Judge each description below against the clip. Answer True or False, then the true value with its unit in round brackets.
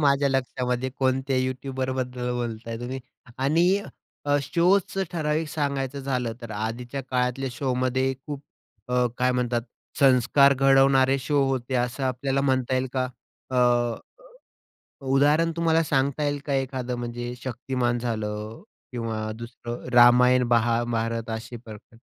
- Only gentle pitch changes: True (2.1 semitones)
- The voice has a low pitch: True (130 Hz)